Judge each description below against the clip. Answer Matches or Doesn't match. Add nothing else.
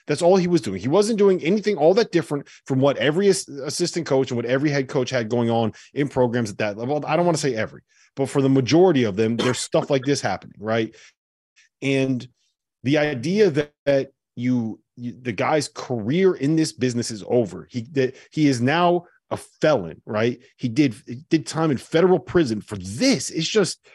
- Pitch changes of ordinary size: Matches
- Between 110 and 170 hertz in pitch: Matches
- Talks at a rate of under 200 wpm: Doesn't match